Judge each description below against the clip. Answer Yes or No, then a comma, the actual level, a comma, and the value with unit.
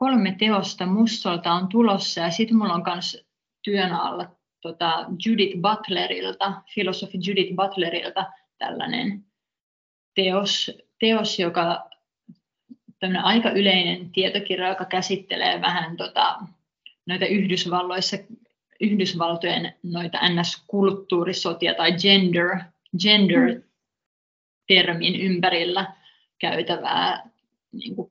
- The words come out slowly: Yes, slow, 90 wpm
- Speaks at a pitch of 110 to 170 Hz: No, high, 190 Hz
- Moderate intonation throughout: No, narrow, 2.3 semitones